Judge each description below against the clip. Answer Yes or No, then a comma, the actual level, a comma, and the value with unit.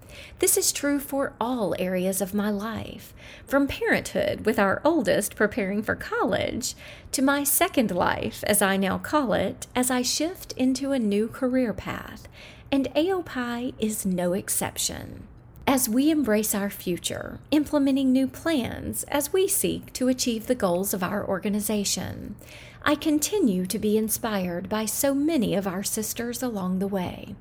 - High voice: Yes, high, 245 Hz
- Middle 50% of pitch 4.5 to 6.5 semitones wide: Yes, wide, 5.5 semitones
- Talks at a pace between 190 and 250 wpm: No, average, 155 wpm